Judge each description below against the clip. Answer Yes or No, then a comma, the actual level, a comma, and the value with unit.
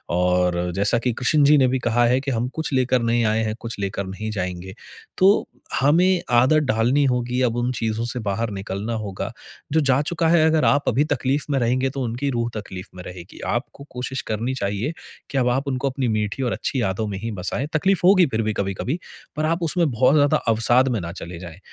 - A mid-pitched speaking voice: No, low, 120 Hz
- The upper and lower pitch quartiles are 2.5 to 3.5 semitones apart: No, average, 4.7 semitones